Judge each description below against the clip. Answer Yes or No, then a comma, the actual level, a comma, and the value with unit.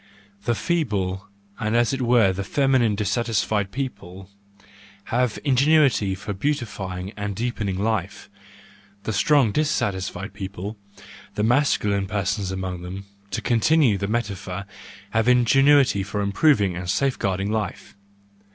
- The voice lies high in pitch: No, low, 105 Hz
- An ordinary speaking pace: No, slow, 115 wpm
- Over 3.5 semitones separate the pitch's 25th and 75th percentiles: Yes, average, 4.0 semitones